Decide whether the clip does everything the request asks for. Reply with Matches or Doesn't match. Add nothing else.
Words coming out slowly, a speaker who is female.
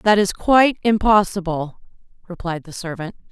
Matches